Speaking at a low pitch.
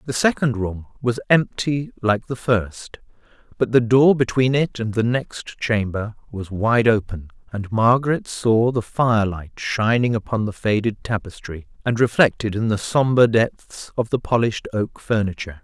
Yes: low, 115 Hz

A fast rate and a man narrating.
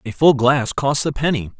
Yes: fast, 225 wpm; male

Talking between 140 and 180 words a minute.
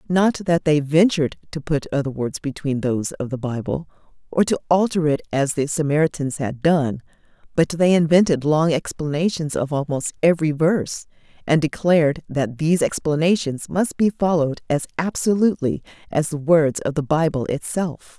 Yes: average, 160 wpm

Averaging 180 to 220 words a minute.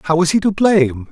No: fast, 270 wpm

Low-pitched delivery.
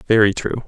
Yes: low, 110 Hz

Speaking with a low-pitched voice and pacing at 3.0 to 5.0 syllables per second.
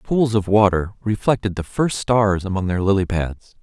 Yes: low, 100 Hz; 4.9 syllables/s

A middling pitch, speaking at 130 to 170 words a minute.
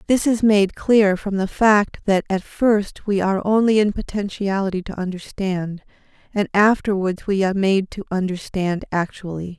No: high, 195 Hz; average, 155 wpm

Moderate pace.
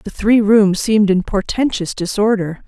Yes: average, 155 wpm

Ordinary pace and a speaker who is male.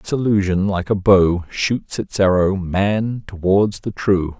Yes: average, 150 wpm; male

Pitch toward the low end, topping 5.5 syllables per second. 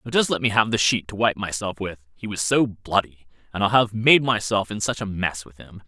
No: low, 100 Hz; 5.3 syllables/s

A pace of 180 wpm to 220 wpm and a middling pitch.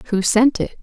No: fast, 215 wpm; high, 230 Hz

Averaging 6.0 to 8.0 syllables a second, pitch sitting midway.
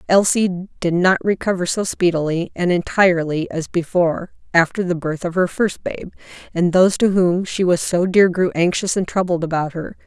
No: 5.2 syllables/s; medium, 180 Hz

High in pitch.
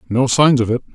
No: low, 120 Hz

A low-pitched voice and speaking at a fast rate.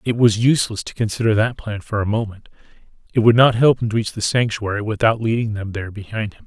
Yes: low, 110 Hz; fast, 225 wpm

